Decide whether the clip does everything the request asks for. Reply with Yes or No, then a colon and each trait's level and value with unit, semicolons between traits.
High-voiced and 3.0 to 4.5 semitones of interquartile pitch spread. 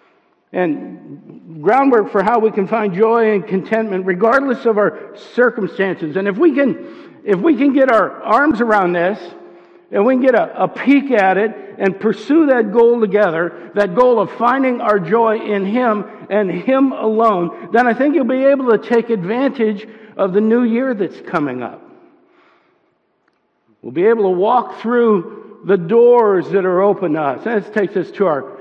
Yes: high, 225 Hz; average, 3.6 semitones